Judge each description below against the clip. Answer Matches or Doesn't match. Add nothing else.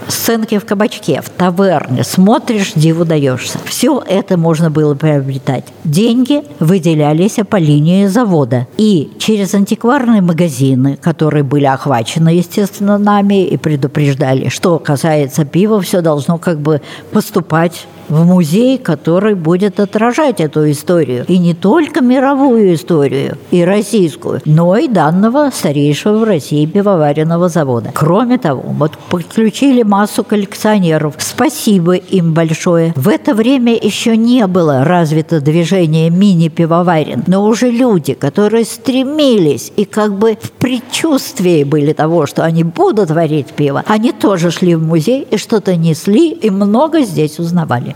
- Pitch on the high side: Doesn't match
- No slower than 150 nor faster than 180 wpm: Doesn't match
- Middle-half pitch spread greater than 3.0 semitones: Matches